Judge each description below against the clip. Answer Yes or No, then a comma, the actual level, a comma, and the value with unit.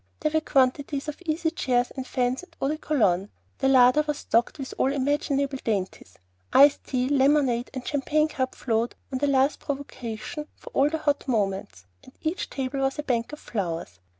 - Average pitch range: Yes, average, 3.2 semitones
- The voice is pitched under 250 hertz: No, very high, 270 Hz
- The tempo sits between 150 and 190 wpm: Yes, average, 185 wpm